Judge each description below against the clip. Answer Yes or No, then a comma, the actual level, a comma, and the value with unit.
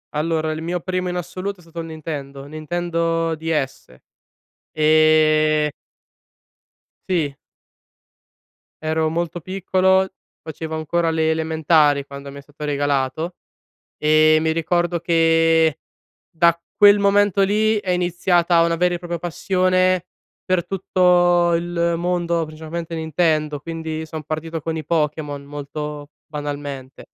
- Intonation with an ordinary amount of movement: No, narrow, 2.2 semitones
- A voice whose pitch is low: No, medium, 165 Hz